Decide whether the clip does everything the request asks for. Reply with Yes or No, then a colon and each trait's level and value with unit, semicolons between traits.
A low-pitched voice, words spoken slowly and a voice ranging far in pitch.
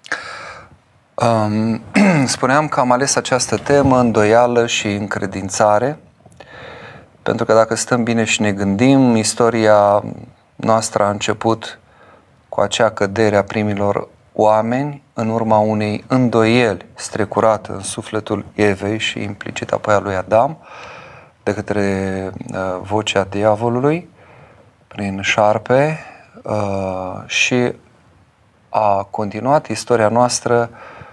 No: low, 110 Hz; slow, 105 wpm; average, 2.9 semitones